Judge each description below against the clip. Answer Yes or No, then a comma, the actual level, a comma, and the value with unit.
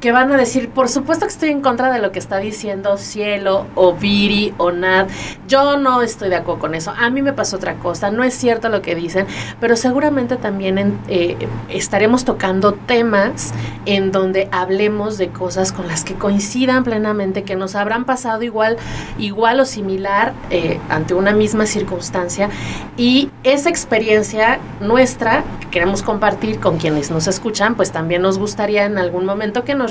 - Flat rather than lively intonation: No, average, 3.8 semitones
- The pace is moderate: Yes, average, 180 wpm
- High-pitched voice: Yes, high, 205 Hz